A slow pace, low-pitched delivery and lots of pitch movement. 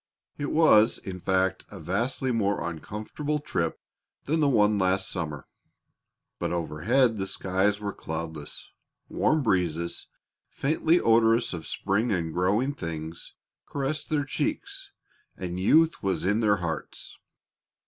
Yes: slow, 130 wpm; low, 100 Hz; wide, 6.2 semitones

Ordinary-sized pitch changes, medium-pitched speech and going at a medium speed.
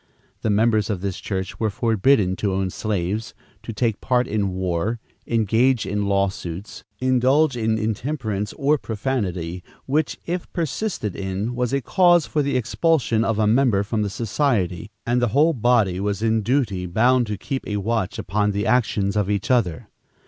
No: average, 4.1 semitones; low, 110 Hz; average, 170 wpm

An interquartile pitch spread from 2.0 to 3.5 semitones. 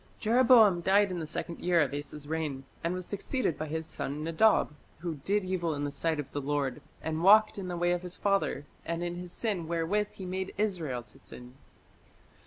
No: average, 4.1 semitones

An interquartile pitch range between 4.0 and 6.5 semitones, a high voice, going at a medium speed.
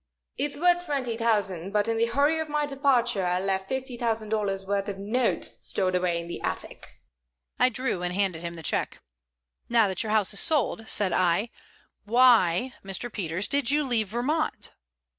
Yes: average, 5.1 semitones; high, 220 Hz; average, 180 wpm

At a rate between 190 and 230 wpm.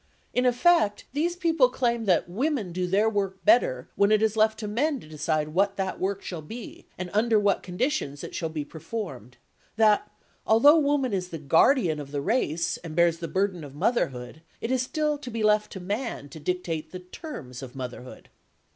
Yes: average, 195 wpm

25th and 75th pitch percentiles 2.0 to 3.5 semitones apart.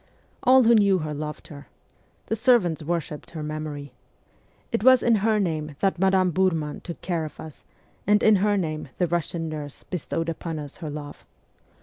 No: average, 4.4 semitones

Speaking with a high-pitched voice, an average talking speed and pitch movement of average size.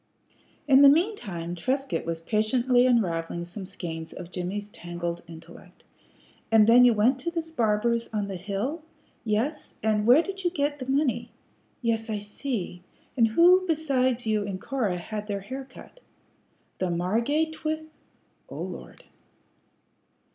No: high, 225 Hz; average, 145 wpm; wide, 6.1 semitones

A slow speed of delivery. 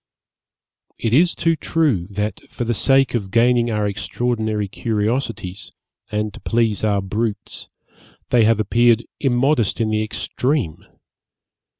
Yes: slow, 125 wpm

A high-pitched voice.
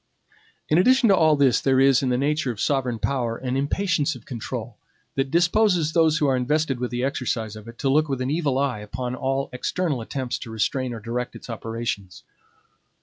No: low, 135 Hz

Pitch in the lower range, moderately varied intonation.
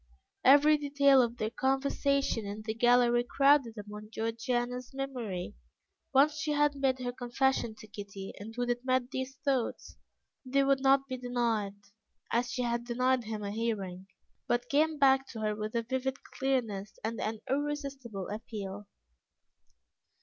No: high, 245 Hz; average, 3.6 semitones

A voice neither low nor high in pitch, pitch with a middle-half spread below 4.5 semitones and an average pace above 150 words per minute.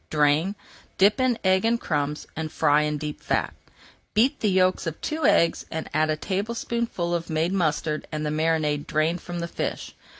Yes: medium, 165 Hz; average, 3.9 semitones; average, 175 wpm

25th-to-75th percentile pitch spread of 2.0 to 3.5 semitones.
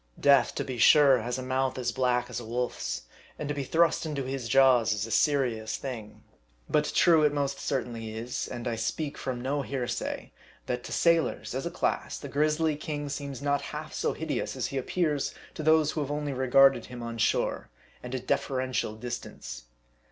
Yes: average, 3.2 semitones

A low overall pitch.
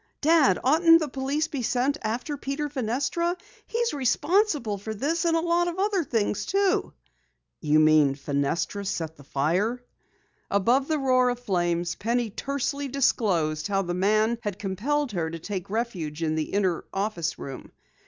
No: high, 230 Hz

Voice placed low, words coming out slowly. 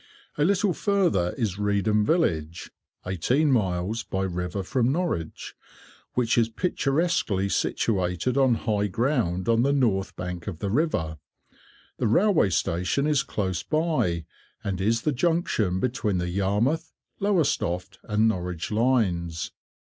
Yes: low, 110 Hz; slow, 120 wpm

